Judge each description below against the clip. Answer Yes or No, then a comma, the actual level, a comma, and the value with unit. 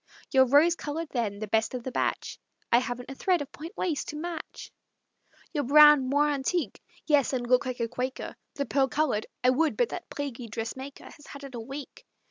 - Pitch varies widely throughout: No, average, 3.2 semitones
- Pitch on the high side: Yes, very high, 270 Hz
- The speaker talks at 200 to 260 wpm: Yes, fast, 205 wpm